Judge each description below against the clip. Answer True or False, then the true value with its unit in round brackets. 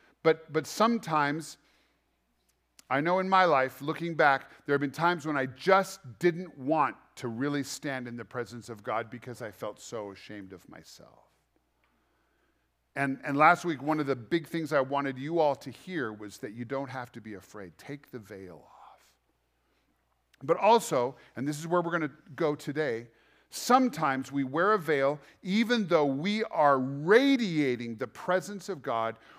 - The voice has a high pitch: False (140 Hz)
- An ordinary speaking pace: True (175 wpm)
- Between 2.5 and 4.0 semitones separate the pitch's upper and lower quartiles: False (5.5 semitones)